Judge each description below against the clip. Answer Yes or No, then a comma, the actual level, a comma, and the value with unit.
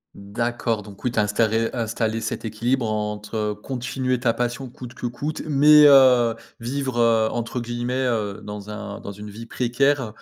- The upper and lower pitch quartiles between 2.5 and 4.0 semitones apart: Yes, average, 2.9 semitones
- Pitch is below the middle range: Yes, low, 115 Hz